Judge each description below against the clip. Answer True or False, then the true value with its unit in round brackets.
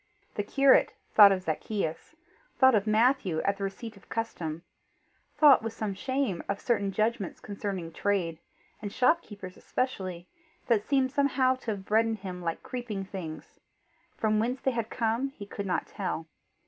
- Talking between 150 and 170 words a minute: True (160 wpm)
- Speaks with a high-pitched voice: True (210 Hz)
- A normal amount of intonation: True (4.1 semitones)